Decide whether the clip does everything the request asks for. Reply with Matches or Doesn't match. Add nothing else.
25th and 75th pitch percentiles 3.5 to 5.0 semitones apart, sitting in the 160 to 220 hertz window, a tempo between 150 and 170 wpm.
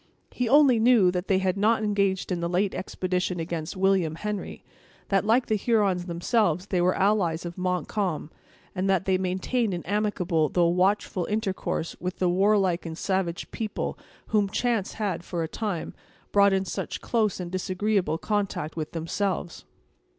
Doesn't match